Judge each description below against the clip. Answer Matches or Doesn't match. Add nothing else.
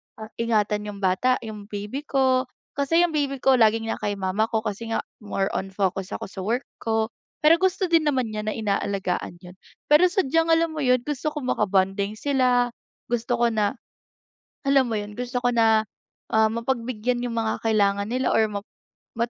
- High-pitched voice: Matches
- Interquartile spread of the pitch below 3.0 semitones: Doesn't match